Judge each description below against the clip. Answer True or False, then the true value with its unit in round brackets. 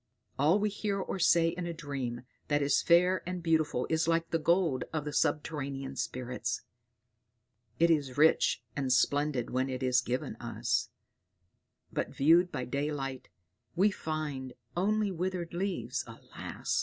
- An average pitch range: True (4.4 semitones)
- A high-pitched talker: False (155 Hz)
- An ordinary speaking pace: True (145 wpm)